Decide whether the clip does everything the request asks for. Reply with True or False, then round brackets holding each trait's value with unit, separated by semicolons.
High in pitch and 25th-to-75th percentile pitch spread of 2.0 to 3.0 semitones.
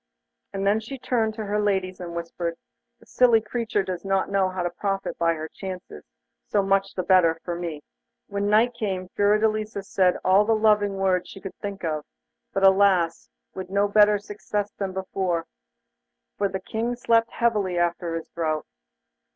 True (195 Hz; 2.5 semitones)